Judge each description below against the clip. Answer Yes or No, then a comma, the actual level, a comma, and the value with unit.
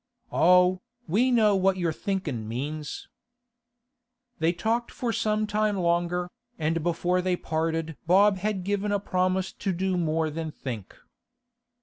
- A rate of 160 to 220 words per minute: No, slow, 135 wpm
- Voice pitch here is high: No, medium, 180 Hz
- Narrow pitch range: No, average, 3.7 semitones